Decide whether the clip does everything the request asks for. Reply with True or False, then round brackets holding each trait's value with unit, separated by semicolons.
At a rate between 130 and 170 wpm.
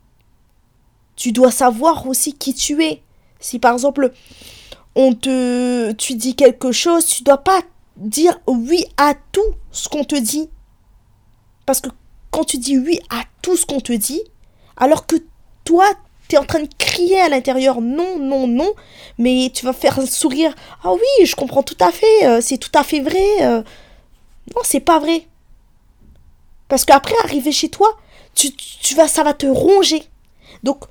False (180 wpm)